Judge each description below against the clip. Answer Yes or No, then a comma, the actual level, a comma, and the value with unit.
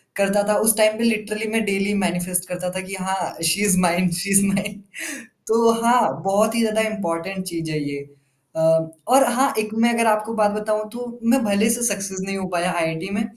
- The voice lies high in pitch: Yes, high, 205 Hz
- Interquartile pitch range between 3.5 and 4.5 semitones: No, average, 3.0 semitones